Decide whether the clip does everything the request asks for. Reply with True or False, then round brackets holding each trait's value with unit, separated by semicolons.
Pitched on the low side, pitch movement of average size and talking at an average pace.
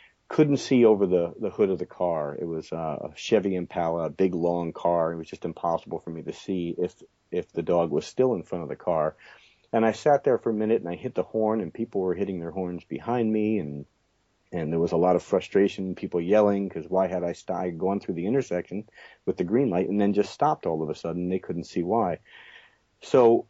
False (95 Hz; 3.9 semitones; 235 wpm)